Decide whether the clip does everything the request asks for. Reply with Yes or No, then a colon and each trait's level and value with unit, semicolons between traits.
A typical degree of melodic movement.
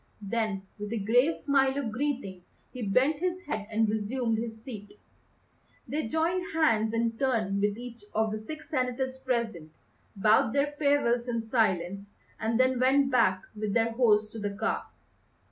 Yes: average, 3.8 semitones